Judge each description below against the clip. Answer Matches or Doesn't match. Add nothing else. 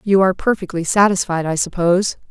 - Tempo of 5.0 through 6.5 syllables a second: Matches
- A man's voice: Doesn't match